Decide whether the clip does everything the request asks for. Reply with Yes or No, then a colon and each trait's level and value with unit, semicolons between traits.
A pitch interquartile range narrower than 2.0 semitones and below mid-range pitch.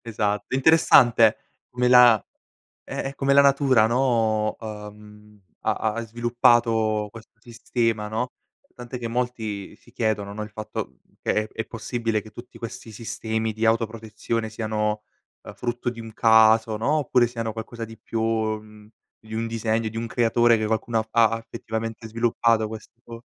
Yes: narrow, 1.5 semitones; low, 115 Hz